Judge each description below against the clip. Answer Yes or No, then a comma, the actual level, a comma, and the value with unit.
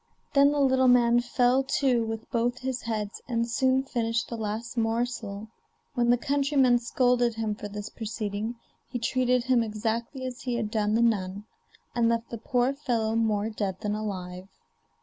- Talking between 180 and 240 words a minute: No, average, 170 wpm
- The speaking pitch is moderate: No, high, 235 Hz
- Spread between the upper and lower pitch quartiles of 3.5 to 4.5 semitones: No, narrow, 2.5 semitones